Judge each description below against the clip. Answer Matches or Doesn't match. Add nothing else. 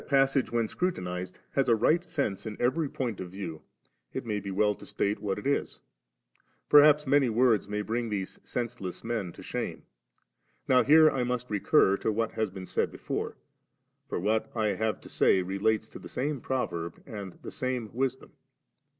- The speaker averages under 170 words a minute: Doesn't match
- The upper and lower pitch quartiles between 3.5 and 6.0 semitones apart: Matches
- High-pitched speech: Doesn't match